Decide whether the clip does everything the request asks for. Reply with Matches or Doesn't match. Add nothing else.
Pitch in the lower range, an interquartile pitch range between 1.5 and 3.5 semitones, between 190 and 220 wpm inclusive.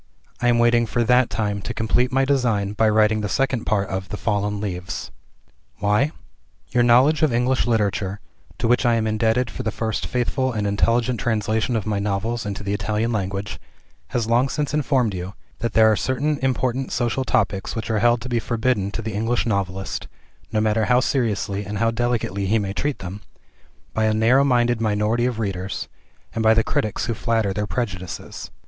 Matches